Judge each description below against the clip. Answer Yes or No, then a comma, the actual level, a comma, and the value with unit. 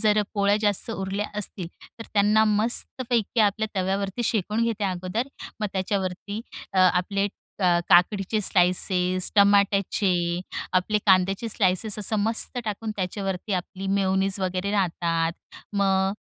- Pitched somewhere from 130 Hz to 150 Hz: No, high, 200 Hz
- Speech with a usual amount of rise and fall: No, narrow, 2.2 semitones